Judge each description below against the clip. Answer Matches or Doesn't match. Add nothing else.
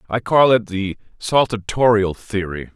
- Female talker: Doesn't match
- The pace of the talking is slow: Matches